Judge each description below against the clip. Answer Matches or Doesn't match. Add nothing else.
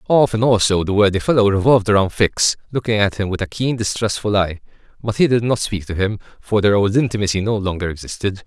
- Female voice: Doesn't match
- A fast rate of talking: Matches